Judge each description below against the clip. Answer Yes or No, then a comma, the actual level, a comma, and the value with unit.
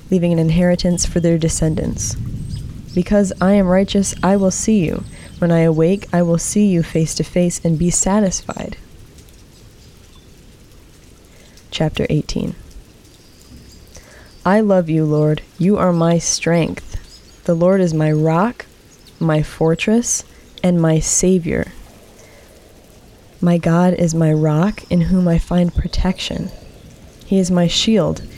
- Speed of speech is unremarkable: No, slow, 130 wpm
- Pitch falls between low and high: Yes, medium, 175 Hz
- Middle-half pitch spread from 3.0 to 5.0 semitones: No, narrow, 2.5 semitones